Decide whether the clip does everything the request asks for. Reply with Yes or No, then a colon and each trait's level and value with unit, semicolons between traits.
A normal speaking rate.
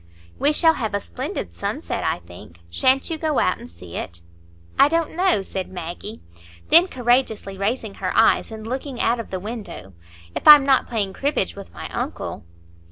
Yes: average, 180 wpm